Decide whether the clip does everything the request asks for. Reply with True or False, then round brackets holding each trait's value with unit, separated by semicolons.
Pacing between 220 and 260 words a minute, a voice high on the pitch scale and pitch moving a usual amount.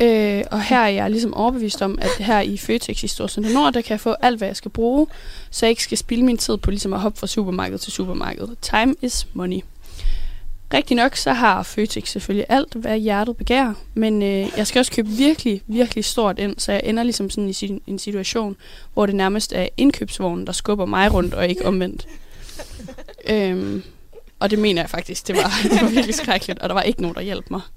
True (225 wpm; 210 Hz; 3.2 semitones)